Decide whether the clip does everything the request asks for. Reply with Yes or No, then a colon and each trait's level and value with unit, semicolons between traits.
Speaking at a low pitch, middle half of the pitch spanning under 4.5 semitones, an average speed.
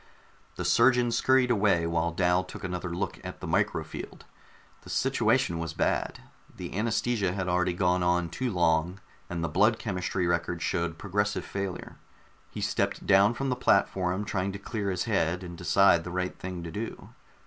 Yes: very low, 90 Hz; average, 2.9 semitones; average, 175 wpm